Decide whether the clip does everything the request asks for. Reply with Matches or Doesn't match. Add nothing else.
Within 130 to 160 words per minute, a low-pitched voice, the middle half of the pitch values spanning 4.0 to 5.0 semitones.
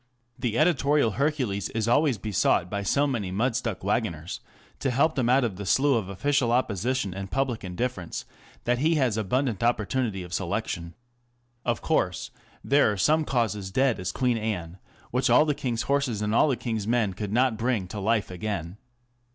Doesn't match